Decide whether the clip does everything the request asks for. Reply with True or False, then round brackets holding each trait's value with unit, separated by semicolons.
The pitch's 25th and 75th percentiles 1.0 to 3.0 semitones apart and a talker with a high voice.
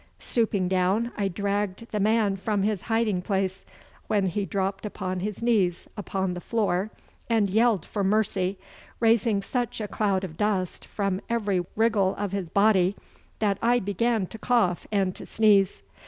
True (2.5 semitones; 200 Hz)